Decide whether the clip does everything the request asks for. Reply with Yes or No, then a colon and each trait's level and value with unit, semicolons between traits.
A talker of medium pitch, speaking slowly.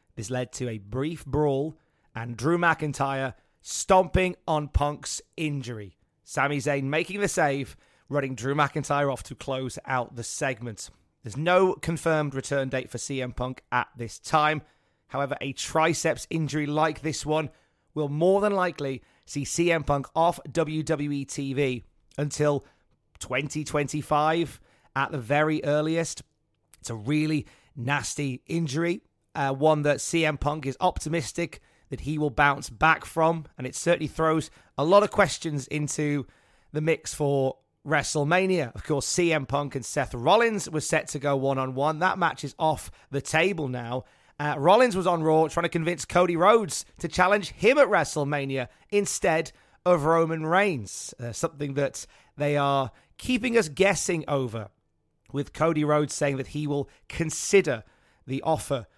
No: medium, 145 Hz; average, 155 wpm